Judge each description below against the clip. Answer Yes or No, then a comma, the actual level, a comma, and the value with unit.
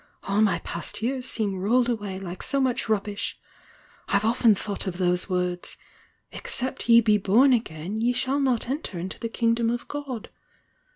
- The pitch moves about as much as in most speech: Yes, average, 4.3 semitones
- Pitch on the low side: No, high, 220 Hz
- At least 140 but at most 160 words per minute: No, average, 170 wpm